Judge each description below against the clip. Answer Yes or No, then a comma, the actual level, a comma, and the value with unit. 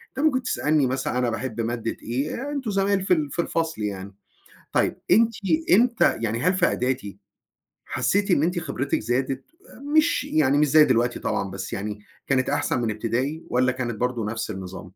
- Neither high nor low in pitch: No, low, 130 Hz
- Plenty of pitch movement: Yes, wide, 6.4 semitones